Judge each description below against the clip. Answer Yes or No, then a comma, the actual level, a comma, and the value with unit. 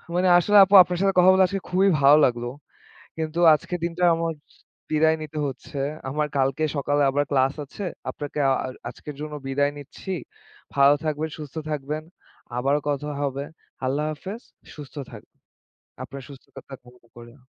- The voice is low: No, medium, 150 Hz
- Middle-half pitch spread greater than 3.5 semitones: No, average, 3.1 semitones